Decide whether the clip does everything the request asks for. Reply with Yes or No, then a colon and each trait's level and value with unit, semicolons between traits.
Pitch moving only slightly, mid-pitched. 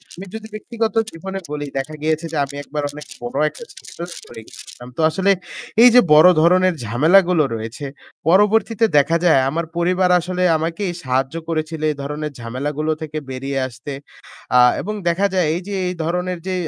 No: average, 4.2 semitones; medium, 160 Hz